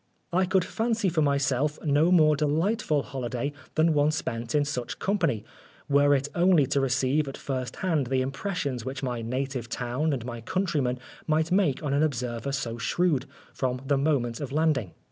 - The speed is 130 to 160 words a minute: No, average, 175 wpm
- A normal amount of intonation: Yes, average, 3.6 semitones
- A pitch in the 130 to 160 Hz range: Yes, medium, 140 Hz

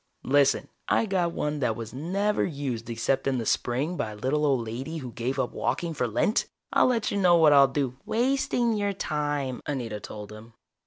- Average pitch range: No, wide, 6.0 semitones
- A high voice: No, medium, 140 Hz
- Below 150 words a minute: No, average, 200 wpm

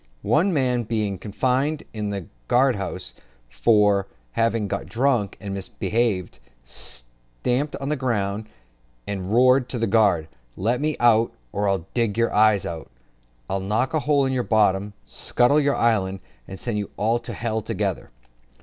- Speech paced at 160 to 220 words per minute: No, average, 150 wpm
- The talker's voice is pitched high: No, low, 110 Hz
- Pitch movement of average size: Yes, average, 4.0 semitones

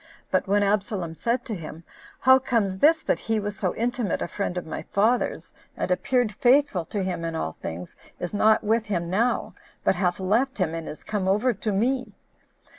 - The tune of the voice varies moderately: Yes, average, 4.5 semitones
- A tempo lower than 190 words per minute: No, average, 200 wpm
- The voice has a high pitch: Yes, high, 205 Hz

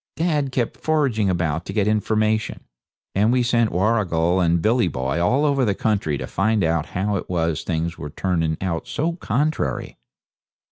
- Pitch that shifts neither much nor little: No, wide, 5.9 semitones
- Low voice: Yes, low, 100 Hz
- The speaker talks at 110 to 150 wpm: No, average, 175 wpm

